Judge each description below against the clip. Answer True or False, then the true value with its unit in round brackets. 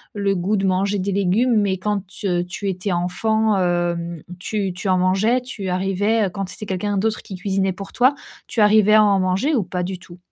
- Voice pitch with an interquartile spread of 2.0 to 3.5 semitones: True (2.4 semitones)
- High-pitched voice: True (195 Hz)